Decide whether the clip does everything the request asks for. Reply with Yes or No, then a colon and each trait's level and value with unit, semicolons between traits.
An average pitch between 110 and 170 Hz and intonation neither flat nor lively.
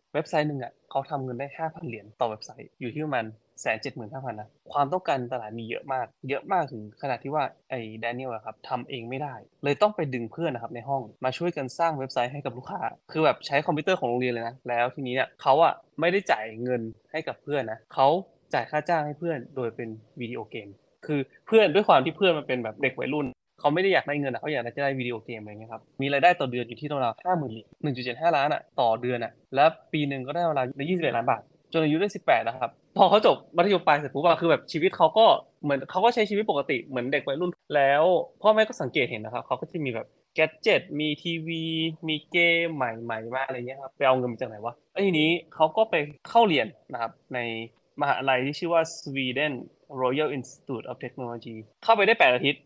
Yes: medium, 140 Hz; average, 4.7 semitones